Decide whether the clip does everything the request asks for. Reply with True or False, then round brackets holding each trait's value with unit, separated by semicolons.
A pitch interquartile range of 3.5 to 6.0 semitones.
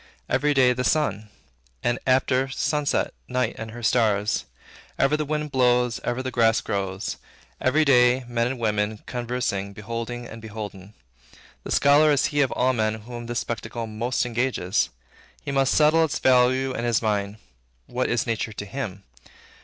False (3.1 semitones)